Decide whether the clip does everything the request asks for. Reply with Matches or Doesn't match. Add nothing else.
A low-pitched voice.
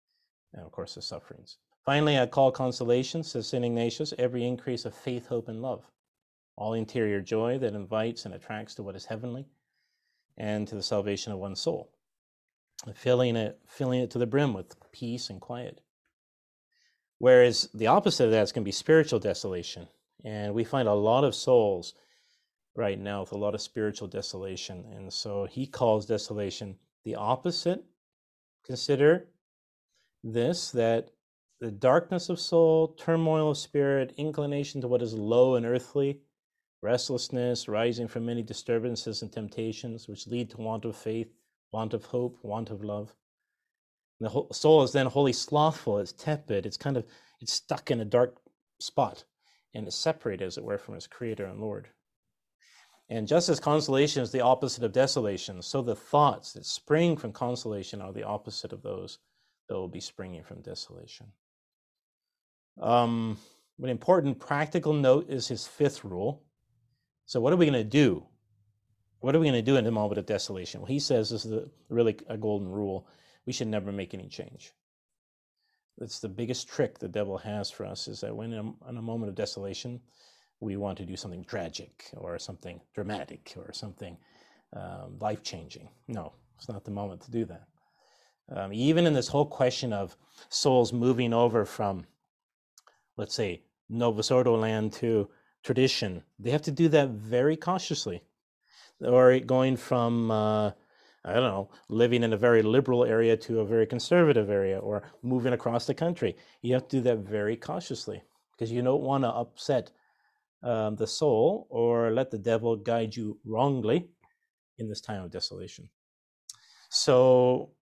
Matches